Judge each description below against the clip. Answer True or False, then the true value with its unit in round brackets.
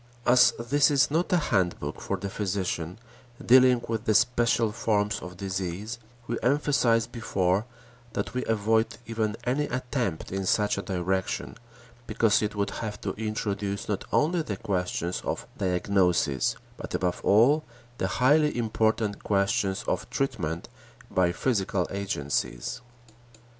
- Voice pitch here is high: False (105 Hz)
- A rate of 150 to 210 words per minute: False (135 wpm)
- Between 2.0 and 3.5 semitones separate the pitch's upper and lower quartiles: False (4.1 semitones)